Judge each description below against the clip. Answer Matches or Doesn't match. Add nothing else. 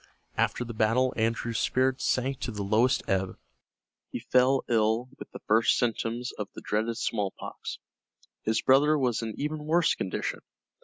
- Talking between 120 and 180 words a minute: Matches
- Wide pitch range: Doesn't match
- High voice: Doesn't match